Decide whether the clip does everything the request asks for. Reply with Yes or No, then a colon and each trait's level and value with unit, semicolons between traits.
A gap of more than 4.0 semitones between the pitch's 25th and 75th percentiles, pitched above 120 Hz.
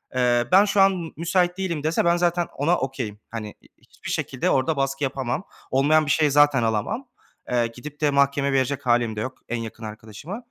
Yes: wide, 5.5 semitones; medium, 140 Hz